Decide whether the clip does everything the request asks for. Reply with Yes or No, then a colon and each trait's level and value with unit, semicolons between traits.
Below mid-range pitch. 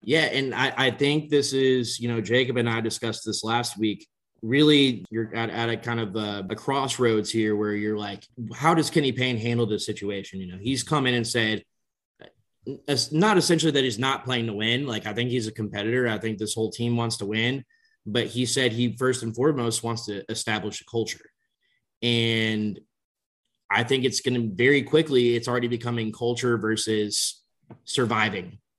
Yes: low, 120 Hz